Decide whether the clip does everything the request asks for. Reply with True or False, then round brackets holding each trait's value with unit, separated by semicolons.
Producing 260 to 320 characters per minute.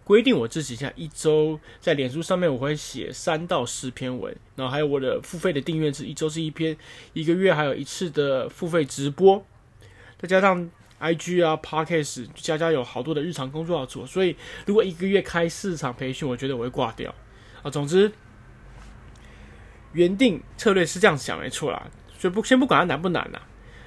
True (295 characters per minute)